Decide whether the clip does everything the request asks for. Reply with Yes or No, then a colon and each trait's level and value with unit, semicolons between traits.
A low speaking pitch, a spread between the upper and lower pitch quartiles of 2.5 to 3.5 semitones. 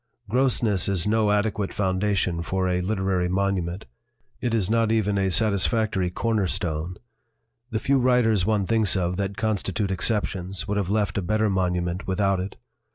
Yes: low, 100 Hz; average, 2.9 semitones